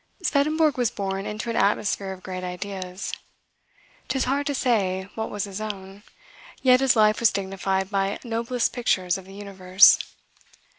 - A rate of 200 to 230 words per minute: No, average, 155 wpm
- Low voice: No, high, 200 Hz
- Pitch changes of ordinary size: Yes, average, 3.7 semitones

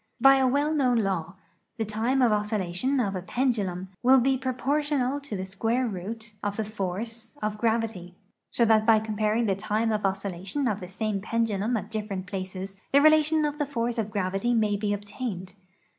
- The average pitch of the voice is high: Yes, high, 220 Hz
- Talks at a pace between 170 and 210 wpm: Yes, average, 185 wpm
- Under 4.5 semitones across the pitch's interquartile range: Yes, average, 4.0 semitones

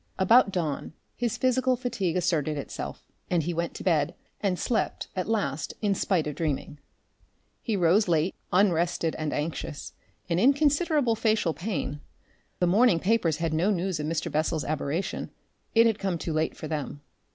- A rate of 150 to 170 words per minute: Yes, average, 165 wpm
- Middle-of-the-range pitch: Yes, medium, 175 Hz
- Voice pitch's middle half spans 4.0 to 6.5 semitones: Yes, wide, 5.5 semitones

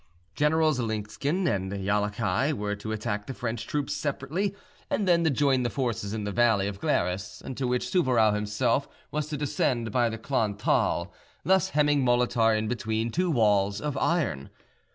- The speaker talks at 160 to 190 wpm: Yes, average, 170 wpm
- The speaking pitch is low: Yes, low, 120 Hz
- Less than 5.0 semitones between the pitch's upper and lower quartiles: No, wide, 5.6 semitones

